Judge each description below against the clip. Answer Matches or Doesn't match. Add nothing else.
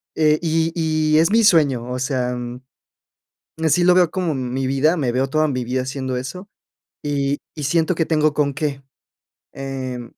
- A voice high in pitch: Doesn't match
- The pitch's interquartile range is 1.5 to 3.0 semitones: Doesn't match